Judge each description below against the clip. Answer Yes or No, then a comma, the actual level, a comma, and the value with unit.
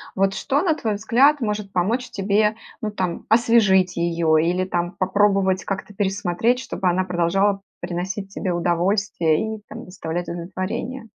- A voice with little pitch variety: No, average, 3.3 semitones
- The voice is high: Yes, high, 195 Hz